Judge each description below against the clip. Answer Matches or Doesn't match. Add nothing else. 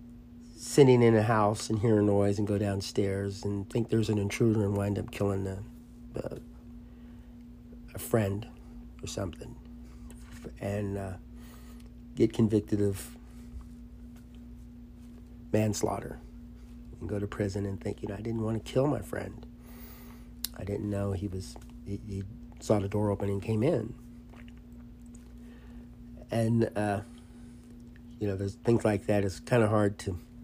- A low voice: Matches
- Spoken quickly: Doesn't match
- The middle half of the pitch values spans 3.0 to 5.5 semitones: Matches